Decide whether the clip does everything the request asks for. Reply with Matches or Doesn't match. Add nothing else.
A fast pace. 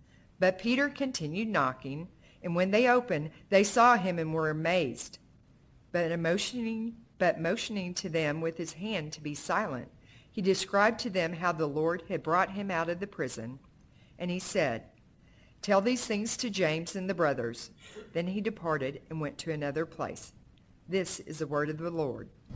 Doesn't match